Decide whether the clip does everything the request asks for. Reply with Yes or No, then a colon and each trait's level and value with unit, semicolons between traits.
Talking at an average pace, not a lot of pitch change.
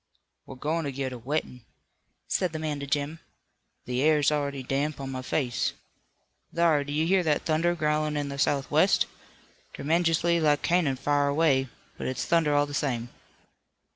Yes: average, 170 wpm; narrow, 2.3 semitones